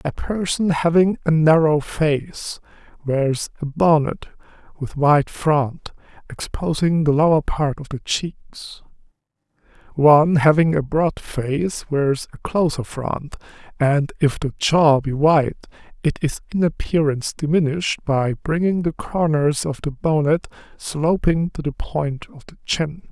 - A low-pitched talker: No, medium, 150 Hz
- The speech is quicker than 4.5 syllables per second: No, 3.9 syllables/s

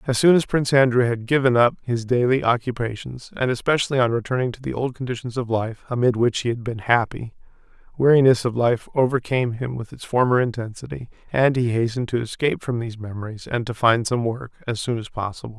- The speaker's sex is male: Yes, male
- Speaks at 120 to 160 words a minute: No, fast, 205 wpm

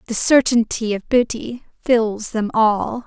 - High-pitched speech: Yes, high, 225 Hz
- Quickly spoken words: No, slow, 135 wpm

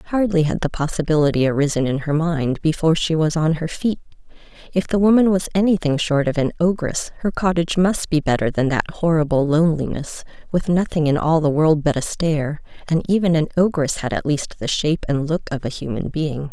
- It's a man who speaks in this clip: No, female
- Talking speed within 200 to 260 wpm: Yes, fast, 205 wpm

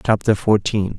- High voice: No, low, 105 Hz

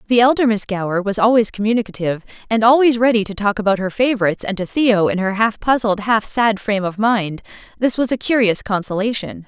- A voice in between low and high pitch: No, high, 215 Hz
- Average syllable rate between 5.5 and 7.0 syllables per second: Yes, 6.0 syllables/s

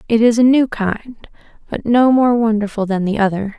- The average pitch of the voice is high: Yes, high, 225 Hz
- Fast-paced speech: No, average, 185 wpm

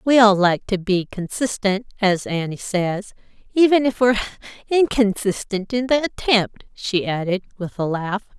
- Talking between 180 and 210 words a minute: No, average, 145 wpm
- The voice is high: Yes, high, 210 Hz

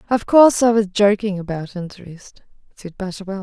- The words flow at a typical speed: Yes, average, 160 wpm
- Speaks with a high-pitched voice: Yes, high, 200 Hz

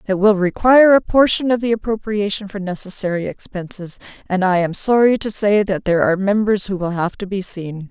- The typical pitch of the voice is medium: No, high, 200 Hz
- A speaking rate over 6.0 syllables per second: No, 5.6 syllables/s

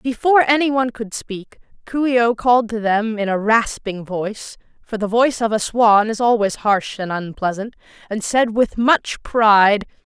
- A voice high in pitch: Yes, high, 225 Hz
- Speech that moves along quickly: No, average, 165 wpm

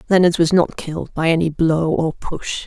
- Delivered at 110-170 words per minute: No, fast, 205 wpm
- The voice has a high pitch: No, medium, 165 Hz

